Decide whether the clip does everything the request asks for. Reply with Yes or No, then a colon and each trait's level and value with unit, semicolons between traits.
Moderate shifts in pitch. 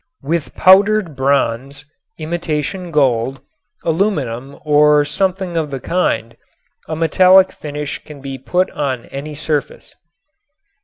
Yes: average, 3.9 semitones